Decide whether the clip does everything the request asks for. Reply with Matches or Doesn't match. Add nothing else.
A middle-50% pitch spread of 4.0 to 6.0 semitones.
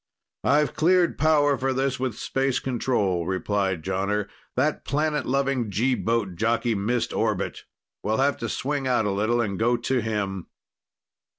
Matches